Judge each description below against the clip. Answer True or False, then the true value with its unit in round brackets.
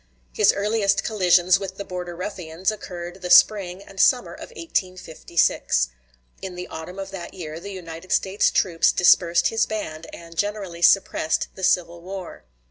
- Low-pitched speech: False (185 Hz)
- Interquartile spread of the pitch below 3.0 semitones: True (2.5 semitones)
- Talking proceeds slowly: False (155 wpm)